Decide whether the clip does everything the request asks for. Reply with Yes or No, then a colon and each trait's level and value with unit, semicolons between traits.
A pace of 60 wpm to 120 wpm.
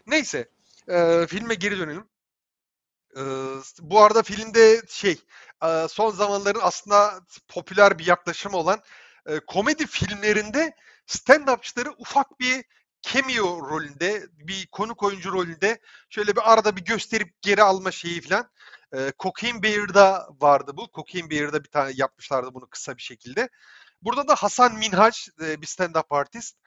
No: average, 135 wpm